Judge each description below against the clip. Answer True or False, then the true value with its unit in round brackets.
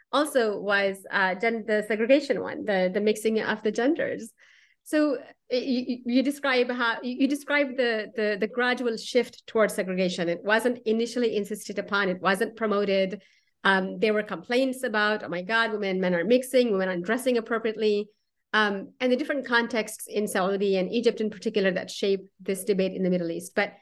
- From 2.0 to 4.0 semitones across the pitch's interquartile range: True (3.5 semitones)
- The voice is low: False (215 Hz)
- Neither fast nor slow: True (180 wpm)